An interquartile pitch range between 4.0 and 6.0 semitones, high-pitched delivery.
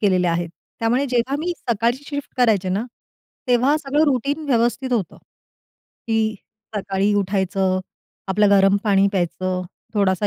Yes: average, 4.5 semitones; high, 210 Hz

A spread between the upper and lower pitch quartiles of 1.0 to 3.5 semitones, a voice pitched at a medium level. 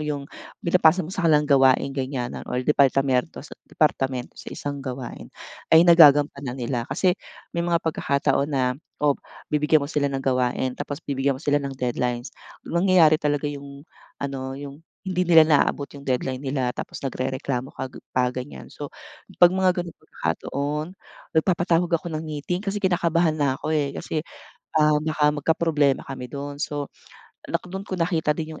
Yes: average, 3.2 semitones; medium, 145 Hz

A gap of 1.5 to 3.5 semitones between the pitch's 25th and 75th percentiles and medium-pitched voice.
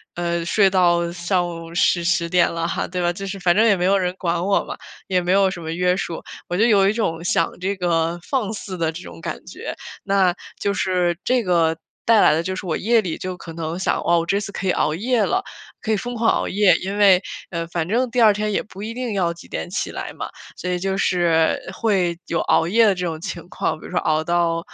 Yes: average, 2.7 semitones; medium, 180 Hz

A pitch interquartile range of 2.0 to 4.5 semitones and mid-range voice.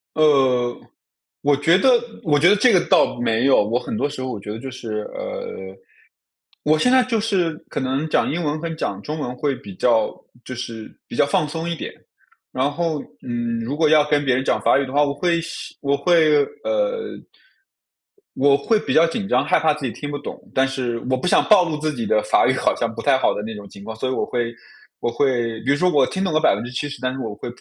No: average, 5.1 semitones; medium, 145 Hz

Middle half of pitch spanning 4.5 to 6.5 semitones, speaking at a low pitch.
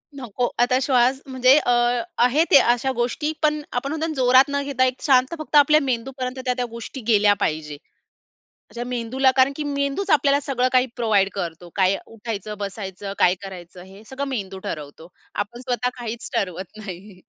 No: average, 4.9 semitones; high, 245 Hz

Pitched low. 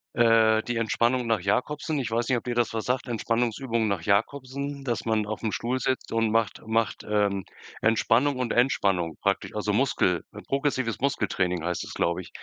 Yes: low, 115 Hz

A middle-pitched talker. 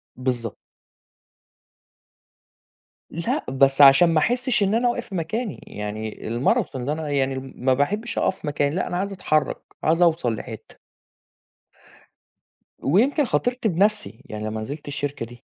Yes: medium, 150 Hz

